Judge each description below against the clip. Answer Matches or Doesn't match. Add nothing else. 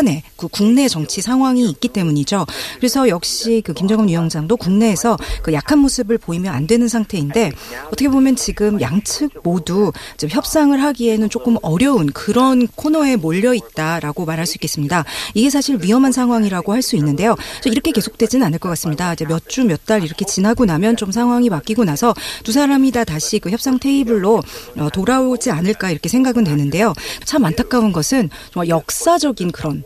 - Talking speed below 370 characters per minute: Doesn't match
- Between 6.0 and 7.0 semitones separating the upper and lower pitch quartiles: Matches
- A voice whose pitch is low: Doesn't match